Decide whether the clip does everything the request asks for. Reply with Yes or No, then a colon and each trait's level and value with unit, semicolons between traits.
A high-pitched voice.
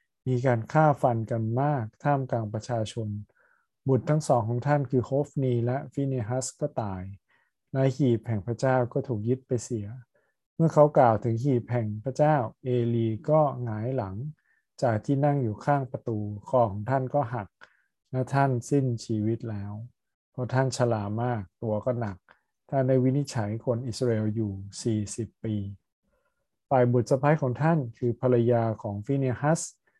No: low, 125 Hz